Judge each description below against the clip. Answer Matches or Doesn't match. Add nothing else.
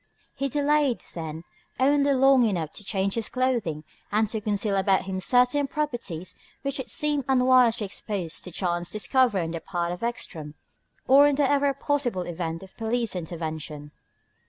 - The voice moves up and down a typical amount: Doesn't match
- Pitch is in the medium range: Doesn't match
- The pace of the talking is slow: Doesn't match